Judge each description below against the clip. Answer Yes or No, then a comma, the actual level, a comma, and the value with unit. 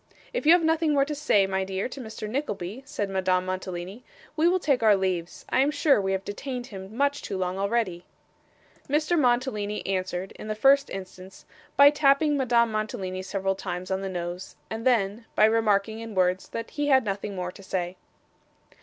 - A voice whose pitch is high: Yes, high, 210 Hz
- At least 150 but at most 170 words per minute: No, average, 190 wpm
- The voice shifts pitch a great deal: Yes, wide, 6.0 semitones